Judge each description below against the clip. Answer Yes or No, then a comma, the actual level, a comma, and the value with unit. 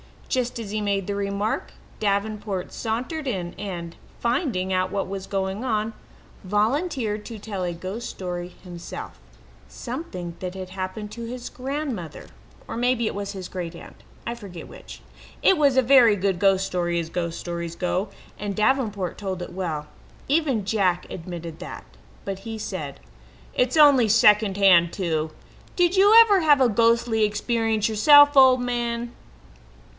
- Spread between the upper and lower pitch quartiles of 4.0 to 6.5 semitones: Yes, average, 4.4 semitones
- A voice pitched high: Yes, high, 205 Hz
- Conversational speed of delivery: Yes, average, 155 wpm